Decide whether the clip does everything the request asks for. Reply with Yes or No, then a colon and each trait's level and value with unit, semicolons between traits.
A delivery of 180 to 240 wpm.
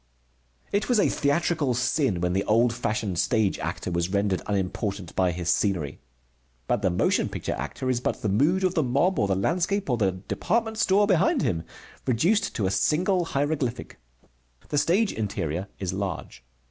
No: average, 170 wpm